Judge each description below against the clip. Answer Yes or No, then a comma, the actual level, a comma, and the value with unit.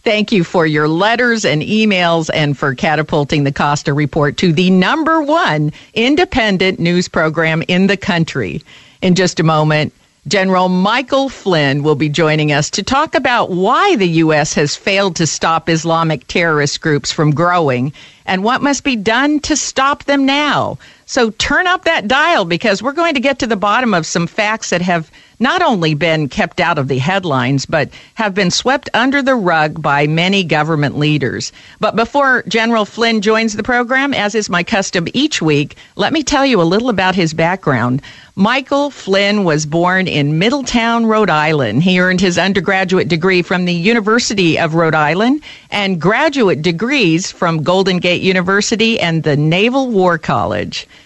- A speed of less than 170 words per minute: No, average, 175 wpm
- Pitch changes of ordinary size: No, wide, 6.2 semitones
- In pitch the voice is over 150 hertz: Yes, medium, 185 Hz